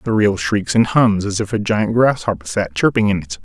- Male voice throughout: Yes, male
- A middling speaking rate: No, fast, 245 wpm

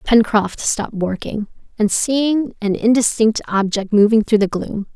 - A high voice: Yes, high, 215 Hz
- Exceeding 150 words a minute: No, average, 145 wpm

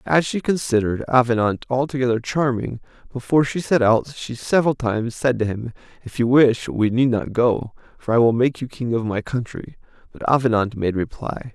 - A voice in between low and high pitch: No, low, 120 Hz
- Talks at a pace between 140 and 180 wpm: No, average, 190 wpm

